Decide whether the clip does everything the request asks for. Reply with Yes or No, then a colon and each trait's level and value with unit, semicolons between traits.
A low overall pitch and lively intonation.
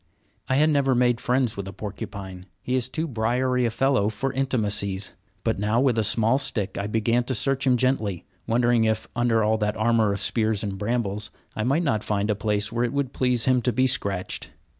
No: low, 115 Hz; average, 3.5 semitones